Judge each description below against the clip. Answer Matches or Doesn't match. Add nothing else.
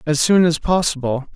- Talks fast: Doesn't match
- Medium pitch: Matches